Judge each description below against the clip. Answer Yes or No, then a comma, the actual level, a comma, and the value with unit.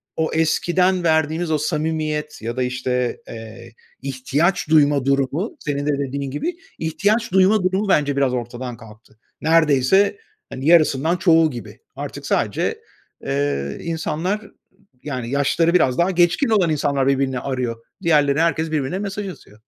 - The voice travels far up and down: No, average, 4.7 semitones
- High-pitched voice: No, medium, 150 Hz